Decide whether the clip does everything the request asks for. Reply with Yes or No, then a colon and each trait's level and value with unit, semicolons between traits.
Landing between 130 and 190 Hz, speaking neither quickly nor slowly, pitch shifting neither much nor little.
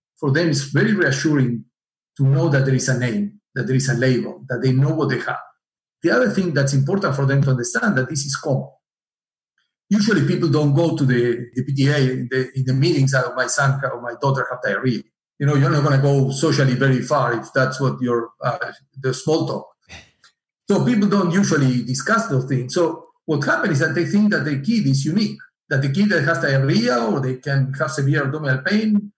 No: medium, 140 Hz; fast, 220 wpm; average, 4.0 semitones